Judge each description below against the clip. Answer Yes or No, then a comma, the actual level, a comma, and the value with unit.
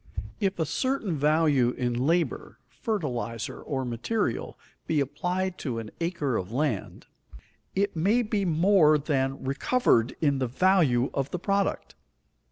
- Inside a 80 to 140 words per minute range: Yes, slow, 135 wpm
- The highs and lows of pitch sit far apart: Yes, wide, 6.3 semitones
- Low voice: No, medium, 155 Hz